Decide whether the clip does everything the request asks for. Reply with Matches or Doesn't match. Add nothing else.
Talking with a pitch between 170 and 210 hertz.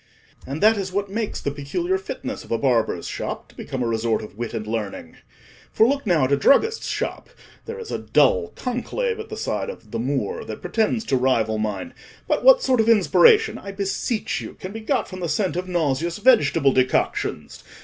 Matches